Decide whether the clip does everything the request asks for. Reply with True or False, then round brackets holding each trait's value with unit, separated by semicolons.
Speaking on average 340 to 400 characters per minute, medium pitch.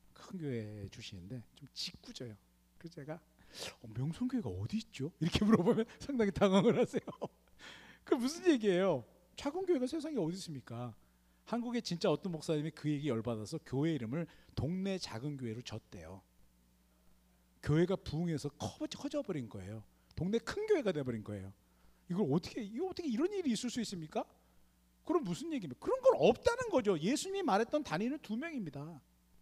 True (360 characters per minute; 160 Hz)